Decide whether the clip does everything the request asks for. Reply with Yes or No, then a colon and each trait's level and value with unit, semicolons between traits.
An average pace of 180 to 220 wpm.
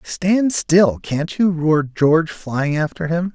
No: average, 160 wpm